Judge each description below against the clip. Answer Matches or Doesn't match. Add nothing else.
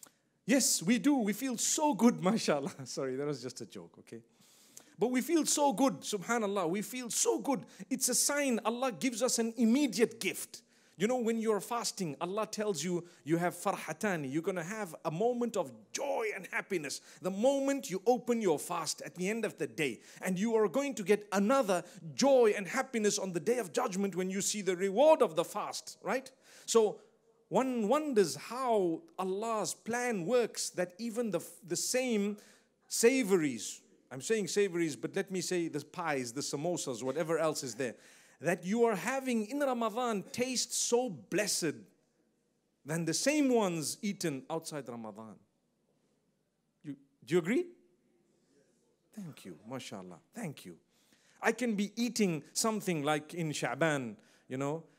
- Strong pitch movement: Matches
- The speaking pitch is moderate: Doesn't match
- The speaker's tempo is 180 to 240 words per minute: Doesn't match